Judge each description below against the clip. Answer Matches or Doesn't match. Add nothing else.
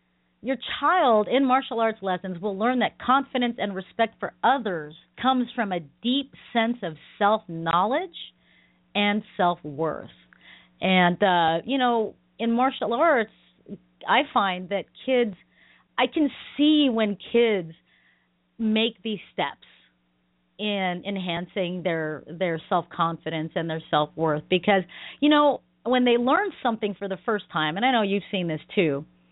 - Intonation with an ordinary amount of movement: Doesn't match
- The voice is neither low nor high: Doesn't match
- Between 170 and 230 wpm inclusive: Doesn't match